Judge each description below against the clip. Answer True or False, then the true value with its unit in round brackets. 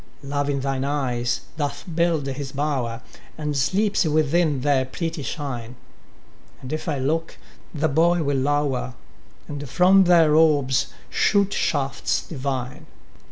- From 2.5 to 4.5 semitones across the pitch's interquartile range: True (3.1 semitones)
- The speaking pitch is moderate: True (145 Hz)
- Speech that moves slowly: True (130 wpm)